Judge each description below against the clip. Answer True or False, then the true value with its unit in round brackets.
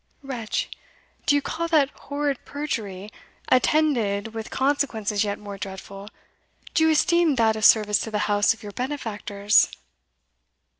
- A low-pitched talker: False (225 Hz)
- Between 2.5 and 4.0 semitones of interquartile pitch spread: False (5.6 semitones)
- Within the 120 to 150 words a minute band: True (140 wpm)